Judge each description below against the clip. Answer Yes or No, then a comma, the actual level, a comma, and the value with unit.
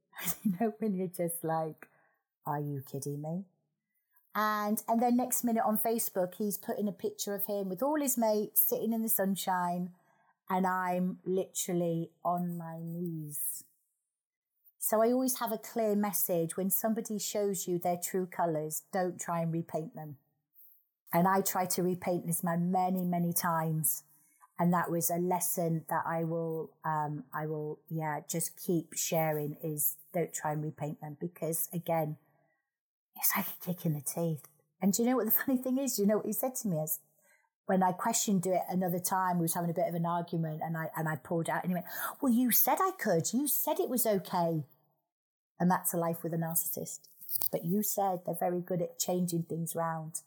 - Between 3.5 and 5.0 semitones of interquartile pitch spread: Yes, average, 3.9 semitones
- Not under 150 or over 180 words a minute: No, average, 195 wpm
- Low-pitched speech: No, medium, 175 Hz